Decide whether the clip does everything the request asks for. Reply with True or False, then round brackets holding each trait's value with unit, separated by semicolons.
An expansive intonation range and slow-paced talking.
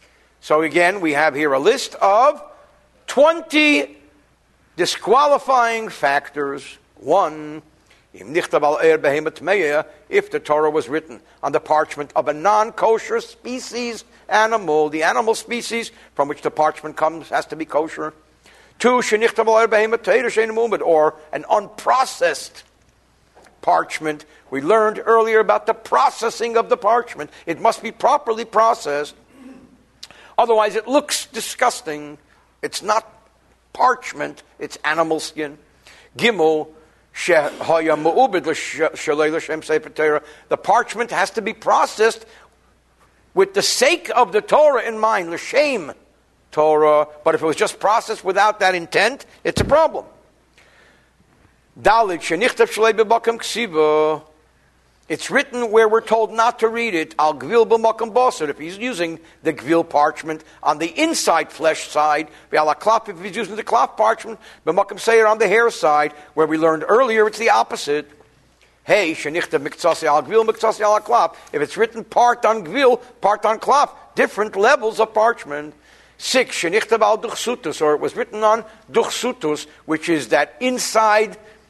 True (6.9 semitones; 115 wpm)